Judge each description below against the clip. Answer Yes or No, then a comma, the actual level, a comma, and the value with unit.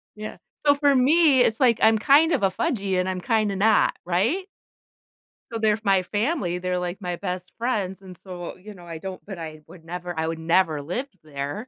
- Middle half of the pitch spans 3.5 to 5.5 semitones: Yes, average, 4.2 semitones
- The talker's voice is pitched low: No, high, 190 Hz